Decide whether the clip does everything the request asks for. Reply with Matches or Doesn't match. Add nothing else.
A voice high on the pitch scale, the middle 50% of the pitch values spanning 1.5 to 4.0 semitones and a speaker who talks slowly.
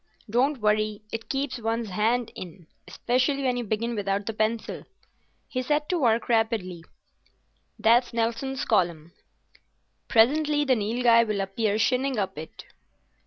Matches